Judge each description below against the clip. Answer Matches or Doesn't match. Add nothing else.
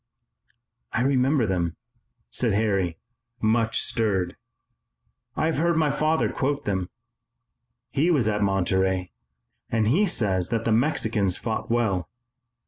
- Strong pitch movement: Matches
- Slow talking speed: Matches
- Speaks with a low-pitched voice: Matches